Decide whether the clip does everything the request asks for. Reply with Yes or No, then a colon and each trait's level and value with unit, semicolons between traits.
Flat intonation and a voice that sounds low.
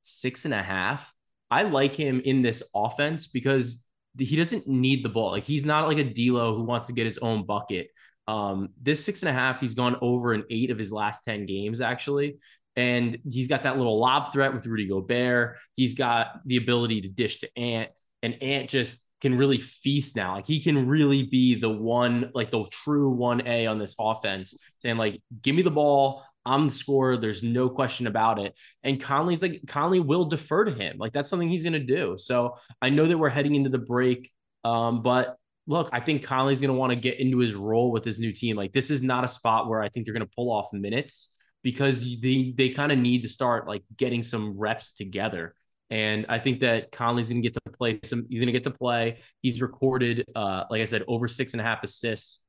No: average, 3.0 semitones; low, 125 Hz